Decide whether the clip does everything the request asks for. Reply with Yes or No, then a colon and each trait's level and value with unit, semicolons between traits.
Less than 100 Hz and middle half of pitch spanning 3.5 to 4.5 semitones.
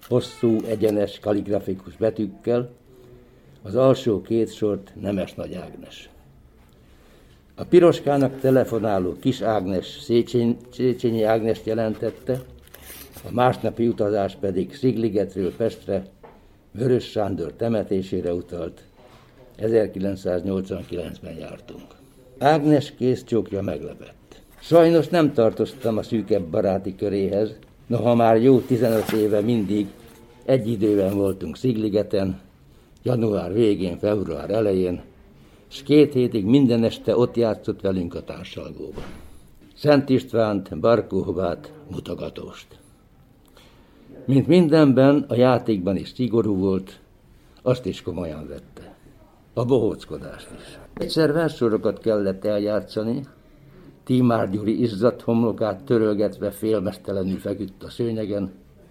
No: low, 110 Hz; average, 4.1 semitones